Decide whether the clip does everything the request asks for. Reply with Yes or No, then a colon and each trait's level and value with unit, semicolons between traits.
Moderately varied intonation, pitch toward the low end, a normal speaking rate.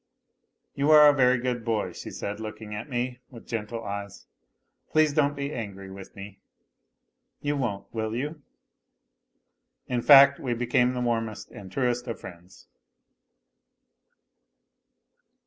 Yes: average, 4.4 semitones; low, 120 Hz; average, 145 wpm